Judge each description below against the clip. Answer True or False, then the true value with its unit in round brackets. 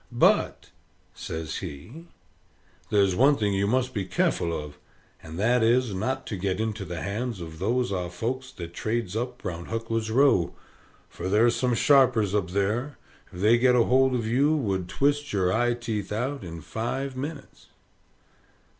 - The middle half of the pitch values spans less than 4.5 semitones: False (5.1 semitones)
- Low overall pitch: True (110 Hz)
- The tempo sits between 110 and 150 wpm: False (165 wpm)